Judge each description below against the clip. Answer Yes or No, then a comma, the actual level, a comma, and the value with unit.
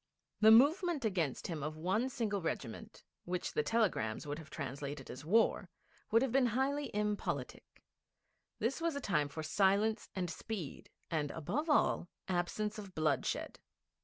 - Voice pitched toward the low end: No, high, 195 Hz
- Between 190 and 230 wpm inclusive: No, average, 150 wpm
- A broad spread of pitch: Yes, wide, 6.8 semitones